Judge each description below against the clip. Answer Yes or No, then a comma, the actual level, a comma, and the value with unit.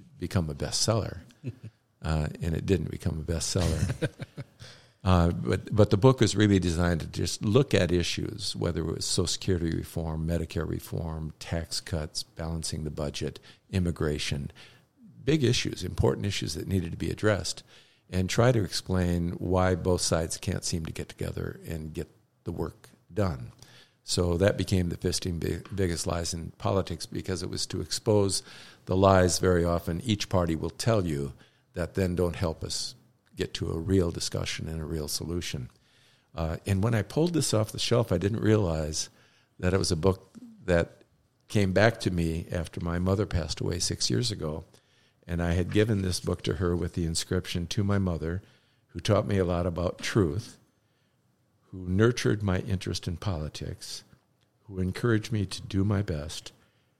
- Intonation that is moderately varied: Yes, average, 4.1 semitones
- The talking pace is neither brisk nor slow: Yes, average, 175 wpm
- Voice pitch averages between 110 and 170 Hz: No, very low, 95 Hz